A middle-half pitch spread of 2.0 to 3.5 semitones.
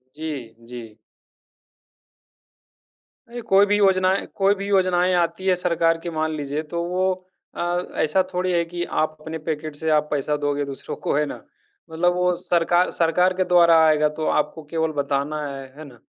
Yes: average, 3.0 semitones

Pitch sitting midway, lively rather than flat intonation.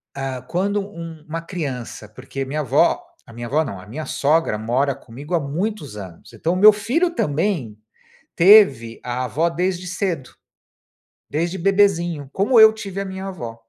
Yes: medium, 165 Hz; wide, 6.5 semitones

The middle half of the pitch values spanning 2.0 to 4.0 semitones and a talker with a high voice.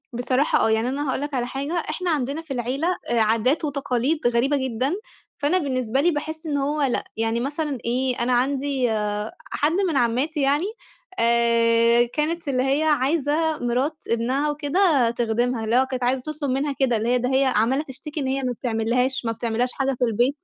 Yes: average, 3.4 semitones; very high, 265 Hz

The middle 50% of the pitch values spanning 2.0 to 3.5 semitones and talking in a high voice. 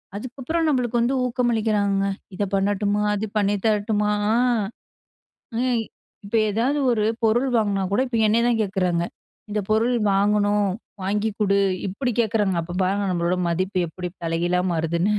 Yes: average, 2.9 semitones; high, 205 Hz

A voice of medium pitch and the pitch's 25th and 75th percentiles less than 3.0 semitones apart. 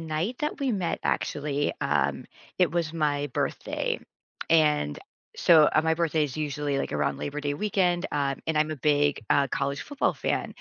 Yes: medium, 150 Hz; narrow, 2.6 semitones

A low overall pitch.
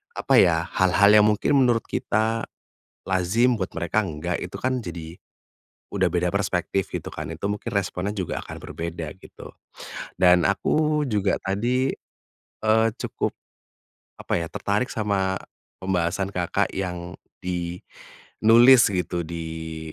Yes: very low, 95 Hz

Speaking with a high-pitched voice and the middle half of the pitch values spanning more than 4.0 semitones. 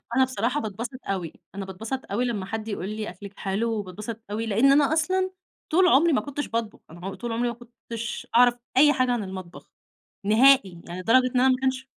Yes: high, 230 Hz; average, 4.4 semitones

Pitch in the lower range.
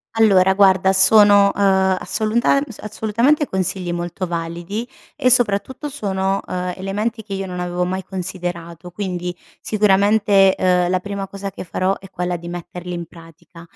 No: high, 190 Hz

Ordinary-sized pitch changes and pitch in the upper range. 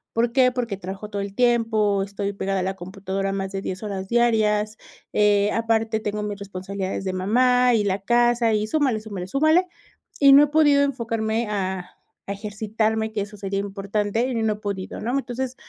Yes: average, 3.2 semitones; high, 210 Hz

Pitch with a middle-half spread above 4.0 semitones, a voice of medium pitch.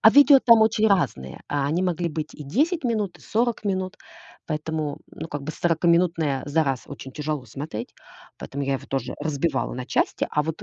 Yes: wide, 5.4 semitones; medium, 160 Hz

